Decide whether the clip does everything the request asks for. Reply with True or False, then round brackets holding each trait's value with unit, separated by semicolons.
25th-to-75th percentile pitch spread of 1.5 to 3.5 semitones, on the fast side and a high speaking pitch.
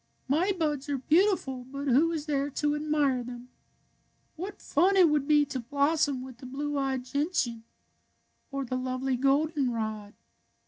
False (2.9 semitones; 155 wpm; 280 Hz)